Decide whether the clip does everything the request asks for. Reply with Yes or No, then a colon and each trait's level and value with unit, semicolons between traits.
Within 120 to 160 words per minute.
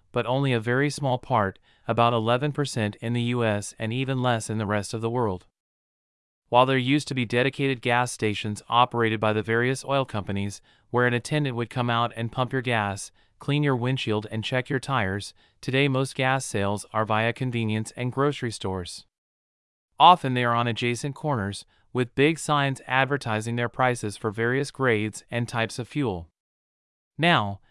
No: average, 175 wpm